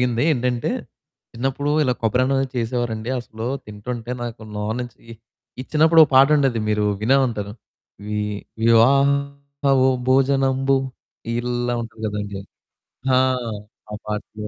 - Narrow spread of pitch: No, average, 3.3 semitones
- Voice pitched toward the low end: Yes, low, 120 Hz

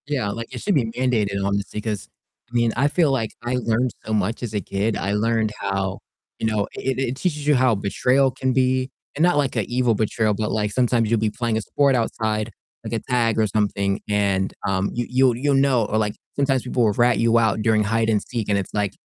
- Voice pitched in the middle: No, low, 115 Hz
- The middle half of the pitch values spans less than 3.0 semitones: No, average, 3.4 semitones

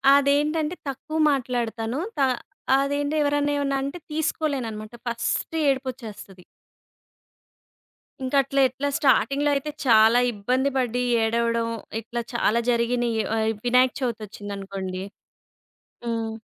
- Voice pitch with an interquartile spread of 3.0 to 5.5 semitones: Yes, average, 3.8 semitones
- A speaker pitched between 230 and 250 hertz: Yes, high, 245 Hz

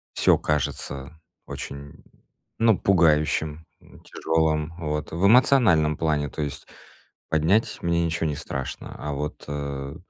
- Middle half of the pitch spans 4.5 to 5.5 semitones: No, narrow, 2.4 semitones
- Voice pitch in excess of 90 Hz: No, very low, 75 Hz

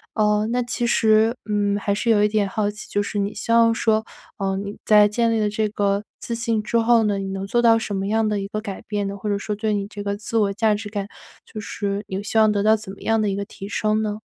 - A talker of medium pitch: No, high, 210 Hz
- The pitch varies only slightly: Yes, narrow, 1.6 semitones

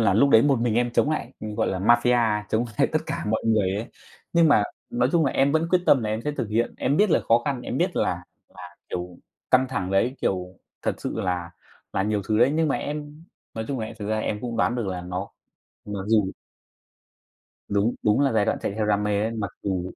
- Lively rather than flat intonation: No, average, 4.0 semitones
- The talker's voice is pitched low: Yes, low, 110 Hz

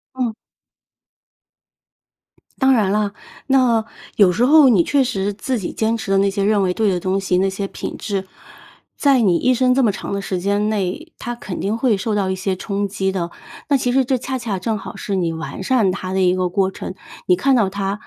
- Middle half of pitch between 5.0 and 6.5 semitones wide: No, average, 4.0 semitones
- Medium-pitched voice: No, high, 200 Hz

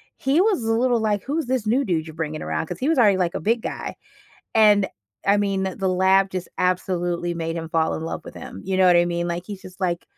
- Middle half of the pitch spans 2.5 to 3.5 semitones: No, average, 3.9 semitones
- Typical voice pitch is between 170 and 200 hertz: Yes, high, 190 Hz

